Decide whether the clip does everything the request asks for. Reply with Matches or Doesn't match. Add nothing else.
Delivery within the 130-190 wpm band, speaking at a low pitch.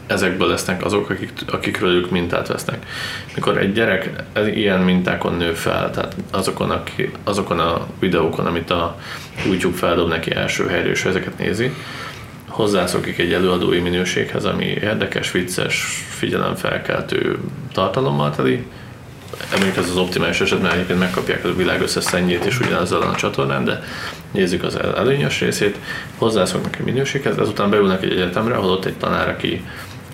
Matches